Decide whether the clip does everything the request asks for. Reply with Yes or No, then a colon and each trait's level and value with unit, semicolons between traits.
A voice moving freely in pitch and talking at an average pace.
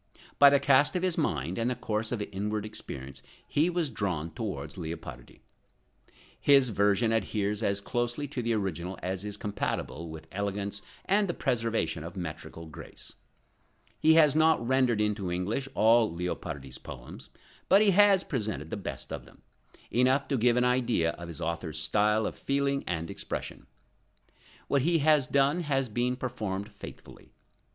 Yes: wide, 6.9 semitones; average, 160 wpm